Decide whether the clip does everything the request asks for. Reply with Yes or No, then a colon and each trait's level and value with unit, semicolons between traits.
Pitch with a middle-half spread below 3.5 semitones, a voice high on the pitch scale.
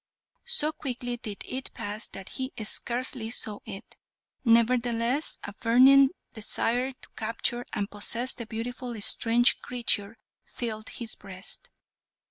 Yes: narrow, 2.5 semitones; high, 235 Hz